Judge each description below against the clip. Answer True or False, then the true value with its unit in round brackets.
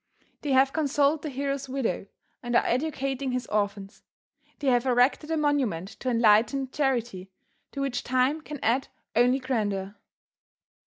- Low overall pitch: False (255 Hz)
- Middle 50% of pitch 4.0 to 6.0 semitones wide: False (3.1 semitones)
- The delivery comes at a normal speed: True (145 wpm)